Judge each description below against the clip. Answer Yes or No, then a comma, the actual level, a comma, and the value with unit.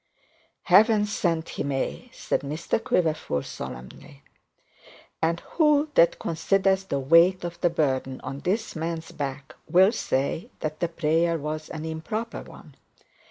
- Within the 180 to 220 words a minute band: No, slow, 135 wpm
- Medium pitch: Yes, medium, 165 Hz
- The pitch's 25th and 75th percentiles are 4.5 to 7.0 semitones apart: No, average, 3.8 semitones